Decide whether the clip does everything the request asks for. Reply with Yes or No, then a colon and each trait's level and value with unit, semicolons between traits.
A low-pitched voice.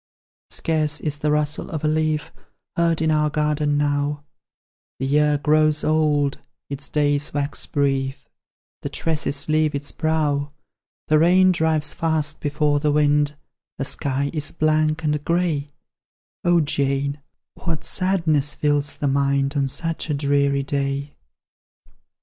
No: medium, 150 Hz